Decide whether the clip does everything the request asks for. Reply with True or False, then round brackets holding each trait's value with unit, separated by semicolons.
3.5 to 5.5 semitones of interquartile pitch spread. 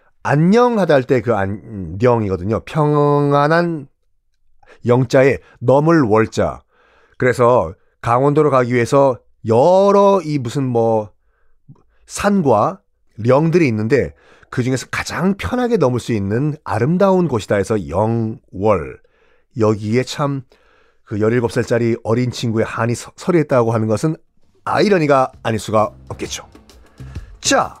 True (5.2 semitones)